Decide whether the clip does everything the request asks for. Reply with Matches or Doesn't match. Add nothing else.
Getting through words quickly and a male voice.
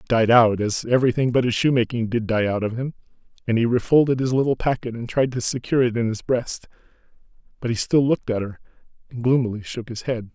Matches